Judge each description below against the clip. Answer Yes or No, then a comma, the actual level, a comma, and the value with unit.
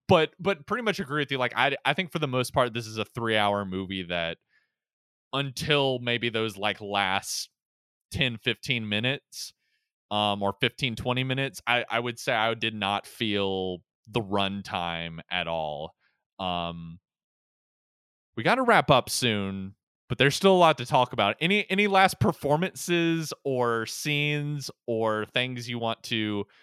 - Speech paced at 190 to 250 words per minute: No, average, 165 wpm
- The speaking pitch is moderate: No, low, 120 Hz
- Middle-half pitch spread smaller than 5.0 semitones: No, wide, 5.6 semitones